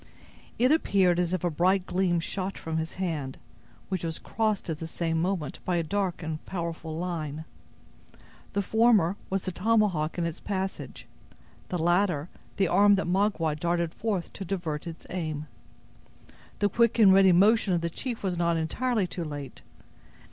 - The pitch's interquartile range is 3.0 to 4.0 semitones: Yes, average, 3.3 semitones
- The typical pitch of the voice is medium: Yes, medium, 180 Hz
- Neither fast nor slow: Yes, average, 170 wpm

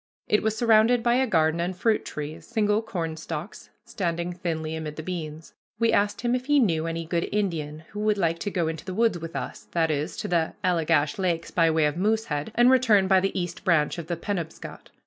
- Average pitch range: Yes, average, 4.7 semitones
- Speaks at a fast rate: Yes, fast, 215 wpm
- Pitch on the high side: No, medium, 175 Hz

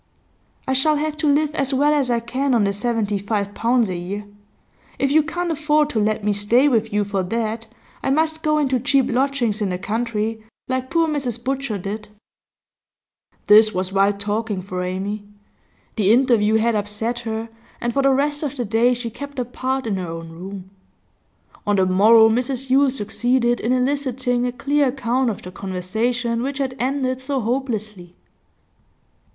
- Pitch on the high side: Yes, high, 235 Hz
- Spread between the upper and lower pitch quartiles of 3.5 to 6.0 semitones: Yes, average, 4.4 semitones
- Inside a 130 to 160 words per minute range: No, average, 180 wpm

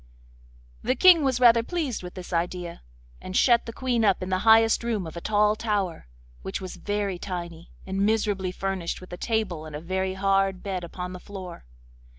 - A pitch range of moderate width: Yes, average, 3.6 semitones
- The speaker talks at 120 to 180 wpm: No, average, 190 wpm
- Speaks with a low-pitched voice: No, high, 195 Hz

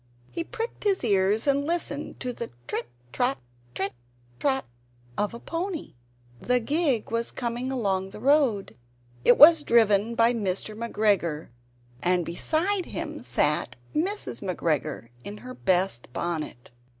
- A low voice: No, high, 235 Hz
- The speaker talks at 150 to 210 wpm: No, slow, 135 wpm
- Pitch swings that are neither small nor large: No, wide, 6.7 semitones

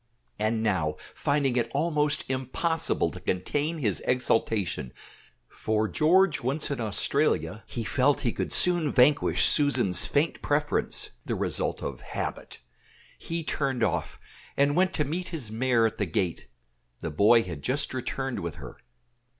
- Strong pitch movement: Yes, wide, 5.7 semitones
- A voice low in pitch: Yes, low, 130 Hz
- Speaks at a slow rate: No, average, 145 wpm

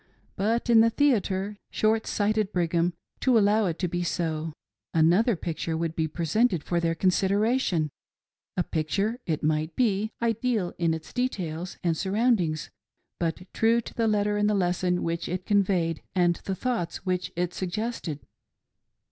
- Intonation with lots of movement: No, average, 4.5 semitones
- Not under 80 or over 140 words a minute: No, average, 165 wpm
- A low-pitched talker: No, medium, 185 Hz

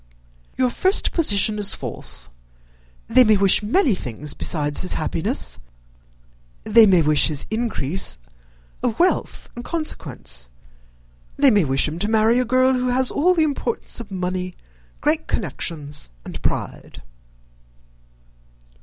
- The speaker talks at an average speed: No, slow, 130 wpm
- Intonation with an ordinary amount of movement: No, wide, 7.5 semitones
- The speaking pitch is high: Yes, high, 210 Hz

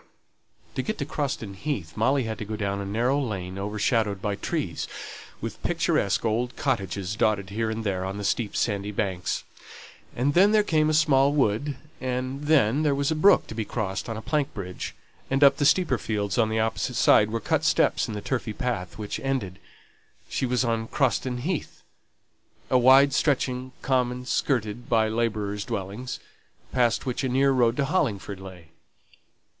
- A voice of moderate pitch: No, low, 115 Hz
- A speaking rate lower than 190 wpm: Yes, average, 180 wpm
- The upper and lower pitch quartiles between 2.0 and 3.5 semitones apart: No, average, 4.8 semitones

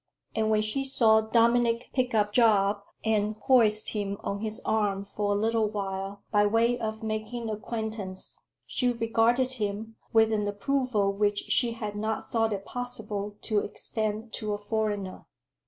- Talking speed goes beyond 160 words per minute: No, average, 155 wpm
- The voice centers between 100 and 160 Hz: No, high, 215 Hz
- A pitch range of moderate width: No, narrow, 1.9 semitones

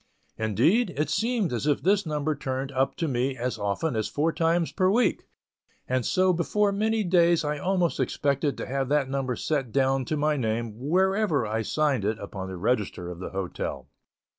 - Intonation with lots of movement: Yes, wide, 5.9 semitones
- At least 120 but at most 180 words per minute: No, average, 190 wpm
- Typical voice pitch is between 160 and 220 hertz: No, medium, 140 Hz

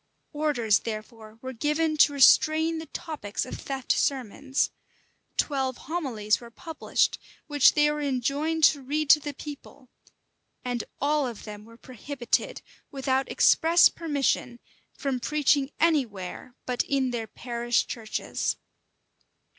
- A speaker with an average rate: No, slow, 130 wpm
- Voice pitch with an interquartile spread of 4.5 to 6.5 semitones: No, average, 3.8 semitones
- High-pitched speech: Yes, very high, 270 Hz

